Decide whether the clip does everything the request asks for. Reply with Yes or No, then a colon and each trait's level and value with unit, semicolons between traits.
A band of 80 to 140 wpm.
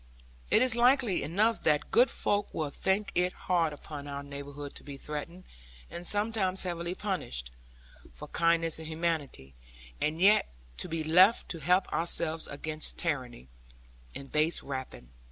No: average, 150 wpm